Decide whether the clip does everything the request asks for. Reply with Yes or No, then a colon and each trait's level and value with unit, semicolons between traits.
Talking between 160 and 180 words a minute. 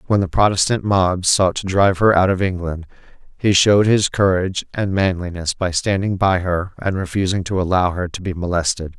No: average, 195 wpm